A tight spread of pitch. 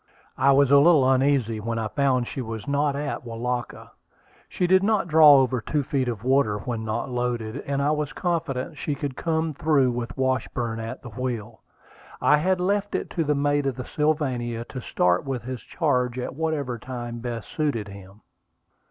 No: average, 3.7 semitones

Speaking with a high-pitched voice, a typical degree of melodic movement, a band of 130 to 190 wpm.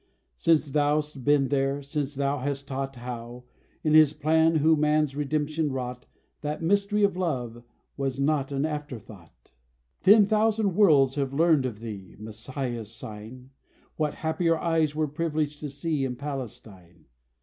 No: medium, 145 Hz; average, 3.4 semitones; average, 145 wpm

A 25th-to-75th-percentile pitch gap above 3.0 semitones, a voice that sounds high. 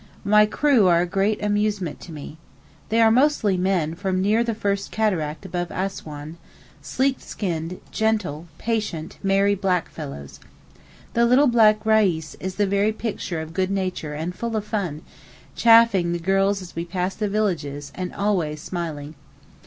Yes: average, 4.1 semitones; high, 195 Hz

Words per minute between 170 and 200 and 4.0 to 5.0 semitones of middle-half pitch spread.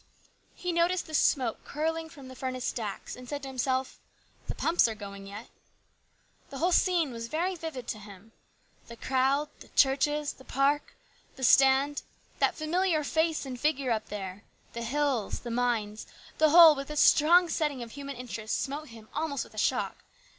Yes: average, 180 wpm; average, 4.6 semitones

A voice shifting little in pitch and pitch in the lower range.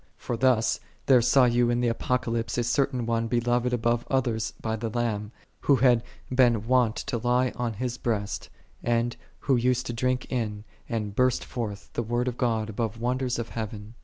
Yes: narrow, 1.7 semitones; low, 120 Hz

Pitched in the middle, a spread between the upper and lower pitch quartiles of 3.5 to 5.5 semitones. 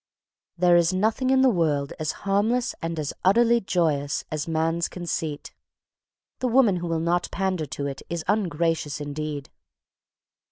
Yes: medium, 170 Hz; average, 4.3 semitones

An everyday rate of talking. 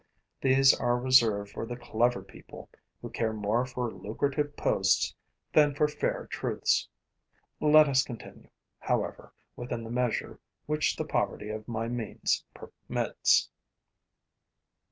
No: slow, 125 wpm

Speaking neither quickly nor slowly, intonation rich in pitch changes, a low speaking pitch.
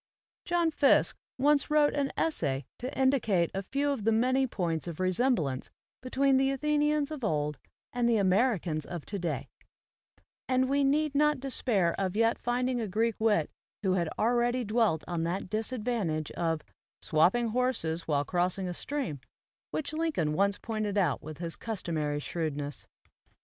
No: average, 160 wpm; wide, 7.5 semitones; high, 220 Hz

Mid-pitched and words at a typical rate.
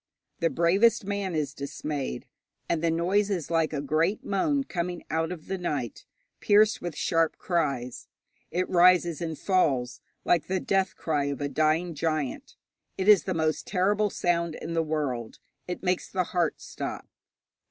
Yes: medium, 170 Hz; average, 165 wpm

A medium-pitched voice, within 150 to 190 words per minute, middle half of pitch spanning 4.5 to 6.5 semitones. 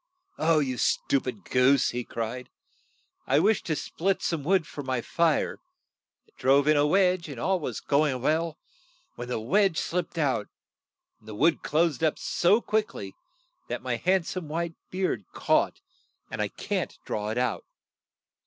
Yes: medium, 150 Hz; average, 170 wpm; average, 5.2 semitones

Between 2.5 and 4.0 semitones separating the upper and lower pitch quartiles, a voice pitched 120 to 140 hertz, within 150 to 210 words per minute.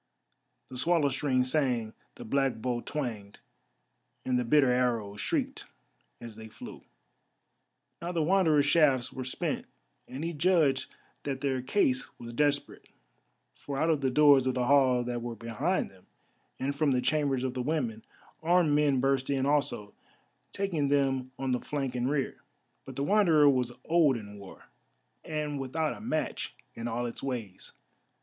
Yes: average, 3.3 semitones; low, 135 Hz; average, 160 wpm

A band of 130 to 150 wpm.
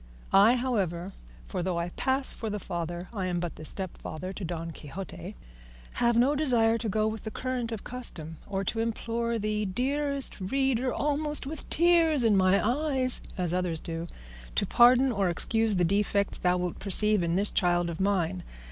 No: average, 180 wpm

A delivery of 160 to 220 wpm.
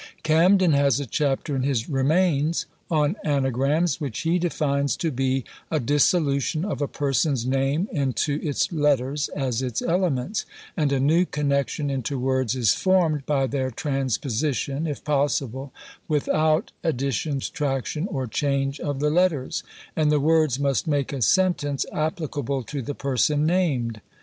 No: average, 145 wpm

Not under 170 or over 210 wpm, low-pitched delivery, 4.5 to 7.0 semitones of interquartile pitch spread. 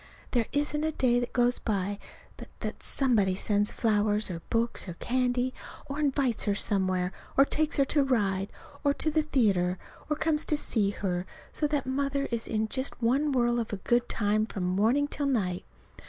No: average, 180 wpm; high, 240 Hz; average, 5.3 semitones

